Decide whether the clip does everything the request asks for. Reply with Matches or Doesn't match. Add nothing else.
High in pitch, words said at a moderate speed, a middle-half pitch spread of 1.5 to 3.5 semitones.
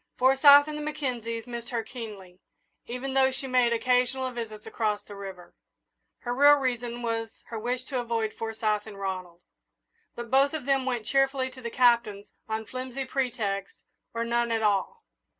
Matches